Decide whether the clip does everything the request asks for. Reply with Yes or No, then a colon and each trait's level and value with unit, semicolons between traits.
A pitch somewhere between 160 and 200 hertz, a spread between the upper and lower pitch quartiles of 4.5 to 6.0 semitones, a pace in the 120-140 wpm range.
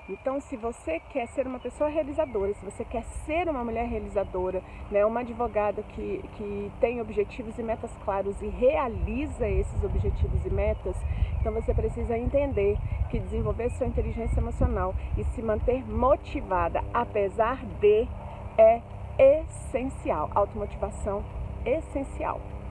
No: high, 225 Hz; average, 5.2 semitones; average, 130 wpm